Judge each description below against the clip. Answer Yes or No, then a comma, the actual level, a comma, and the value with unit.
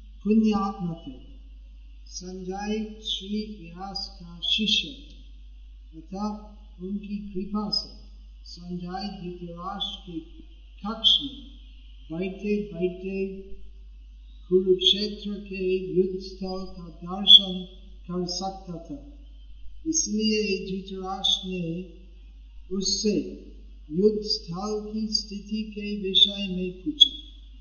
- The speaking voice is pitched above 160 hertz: Yes, high, 190 Hz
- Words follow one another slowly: Yes, slow, 75 wpm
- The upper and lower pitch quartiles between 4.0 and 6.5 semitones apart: No, average, 2.8 semitones